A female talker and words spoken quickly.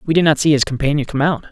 No: male; fast, 320 wpm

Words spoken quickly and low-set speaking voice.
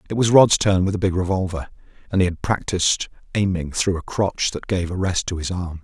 Yes: fast, 235 wpm; very low, 95 Hz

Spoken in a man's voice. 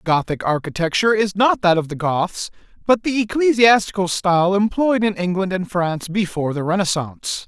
Yes: male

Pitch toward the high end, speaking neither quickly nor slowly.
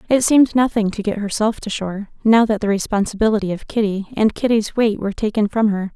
No: high, 215 Hz; fast, 210 wpm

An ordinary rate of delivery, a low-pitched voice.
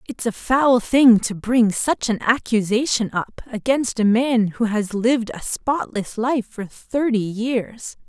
No: average, 165 wpm; high, 230 Hz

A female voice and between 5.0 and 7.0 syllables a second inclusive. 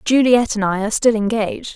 Yes: female; 6.1 syllables/s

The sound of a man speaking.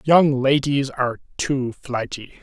Yes: male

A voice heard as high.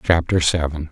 No: very low, 80 Hz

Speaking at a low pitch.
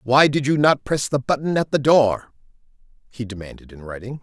Yes: low, 130 Hz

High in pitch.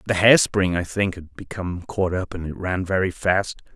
No: very low, 90 Hz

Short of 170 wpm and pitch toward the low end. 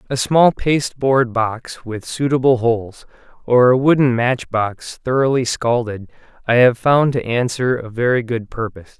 Yes: average, 160 wpm; low, 125 Hz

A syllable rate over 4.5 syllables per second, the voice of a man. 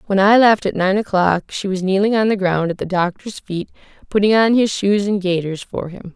No: 5.2 syllables/s; female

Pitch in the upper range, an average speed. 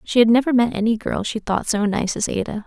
No: high, 220 Hz; fast, 270 wpm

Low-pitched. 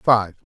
Yes: low, 105 Hz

